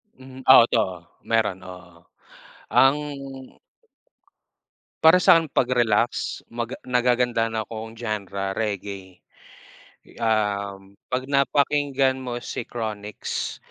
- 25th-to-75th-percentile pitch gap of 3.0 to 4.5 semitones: Yes, average, 4.2 semitones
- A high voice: No, low, 115 Hz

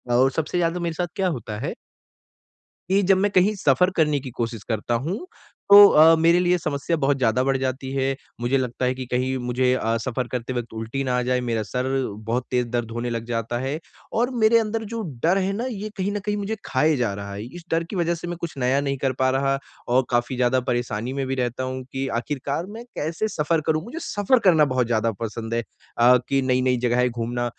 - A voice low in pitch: Yes, low, 130 Hz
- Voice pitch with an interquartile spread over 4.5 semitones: Yes, wide, 5.5 semitones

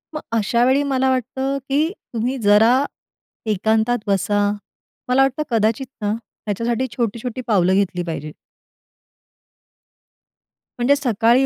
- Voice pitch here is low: No, high, 235 Hz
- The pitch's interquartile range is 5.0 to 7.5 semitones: No, average, 4.1 semitones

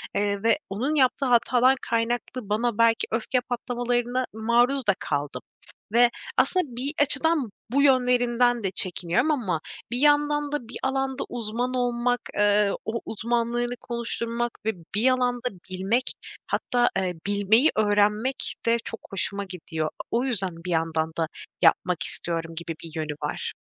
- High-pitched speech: Yes, high, 235 Hz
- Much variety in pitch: No, average, 3.7 semitones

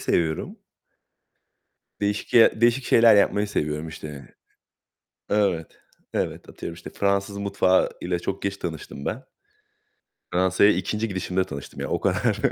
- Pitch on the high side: No, very low, 95 Hz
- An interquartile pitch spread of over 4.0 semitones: No, average, 3.4 semitones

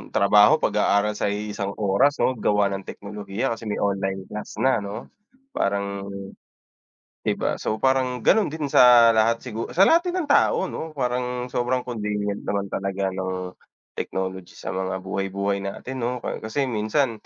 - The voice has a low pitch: Yes, low, 105 Hz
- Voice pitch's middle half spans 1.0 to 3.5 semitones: No, average, 4.1 semitones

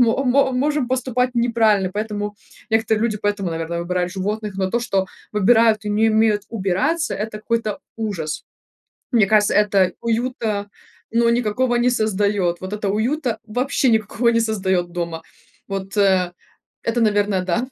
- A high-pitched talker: Yes, high, 215 Hz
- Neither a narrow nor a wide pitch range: Yes, average, 3.2 semitones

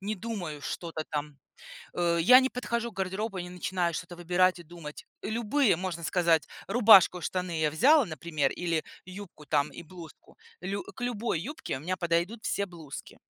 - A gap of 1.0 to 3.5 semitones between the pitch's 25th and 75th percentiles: No, average, 3.9 semitones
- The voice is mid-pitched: Yes, medium, 180 Hz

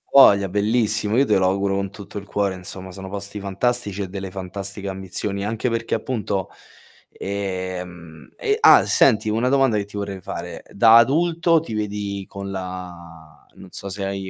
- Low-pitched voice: Yes, low, 100 Hz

